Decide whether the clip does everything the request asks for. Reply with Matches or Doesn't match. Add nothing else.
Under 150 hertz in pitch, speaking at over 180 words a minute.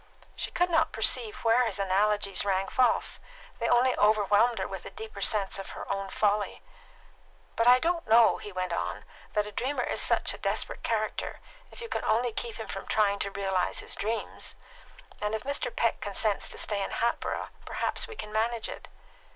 Doesn't match